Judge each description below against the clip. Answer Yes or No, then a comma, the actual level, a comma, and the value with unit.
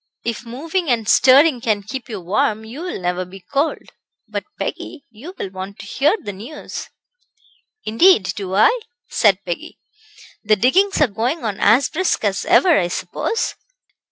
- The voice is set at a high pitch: Yes, high, 230 Hz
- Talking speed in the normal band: Yes, average, 160 wpm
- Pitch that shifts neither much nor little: No, wide, 7.2 semitones